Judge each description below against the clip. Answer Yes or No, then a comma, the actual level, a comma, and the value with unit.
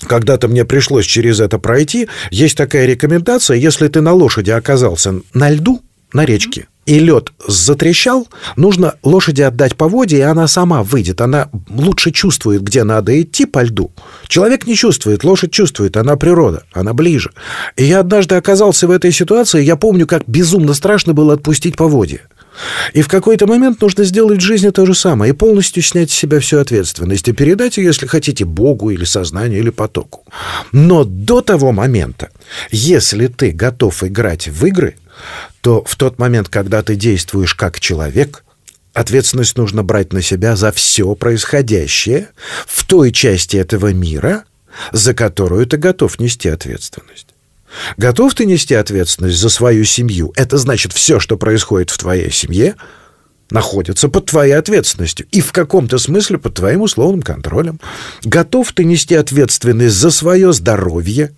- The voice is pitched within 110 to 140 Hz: Yes, low, 135 Hz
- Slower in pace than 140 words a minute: No, fast, 160 wpm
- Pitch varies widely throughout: Yes, wide, 8.1 semitones